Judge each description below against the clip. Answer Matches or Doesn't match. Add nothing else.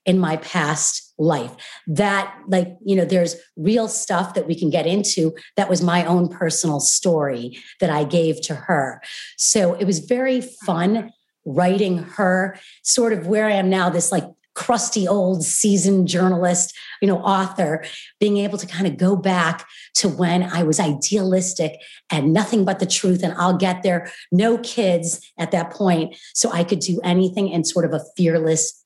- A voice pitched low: Doesn't match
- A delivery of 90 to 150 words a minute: Doesn't match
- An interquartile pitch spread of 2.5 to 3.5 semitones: Matches